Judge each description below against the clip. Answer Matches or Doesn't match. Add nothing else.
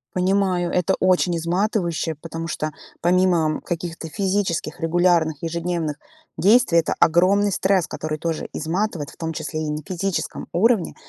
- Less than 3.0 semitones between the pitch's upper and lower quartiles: Matches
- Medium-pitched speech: Matches